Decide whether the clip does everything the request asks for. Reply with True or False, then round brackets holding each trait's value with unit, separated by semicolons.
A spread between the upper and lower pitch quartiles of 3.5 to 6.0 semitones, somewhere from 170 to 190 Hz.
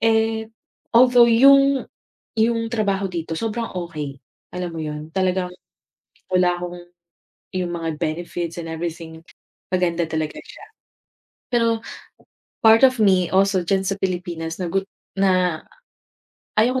True (4.7 semitones; 185 Hz)